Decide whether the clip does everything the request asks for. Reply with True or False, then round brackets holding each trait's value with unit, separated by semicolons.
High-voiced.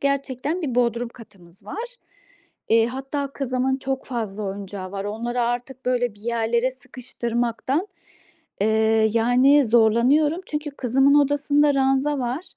True (245 Hz)